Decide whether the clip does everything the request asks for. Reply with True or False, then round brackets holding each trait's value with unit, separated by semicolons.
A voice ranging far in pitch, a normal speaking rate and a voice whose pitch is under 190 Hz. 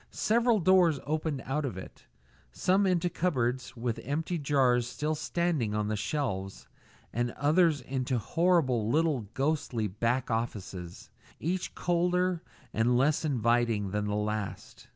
False (6.3 semitones; 130 wpm; 135 Hz)